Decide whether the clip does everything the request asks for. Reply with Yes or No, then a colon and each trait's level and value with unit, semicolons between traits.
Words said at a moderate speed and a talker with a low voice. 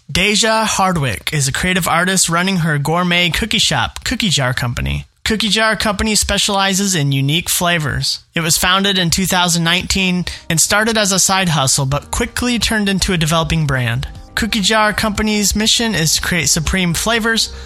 No: average, 165 wpm; medium, 185 Hz